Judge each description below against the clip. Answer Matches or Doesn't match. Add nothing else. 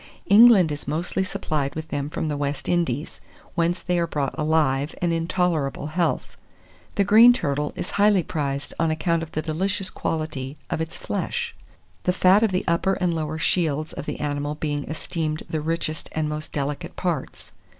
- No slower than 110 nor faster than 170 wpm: Doesn't match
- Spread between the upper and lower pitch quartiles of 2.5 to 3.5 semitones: Matches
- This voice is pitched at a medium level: Matches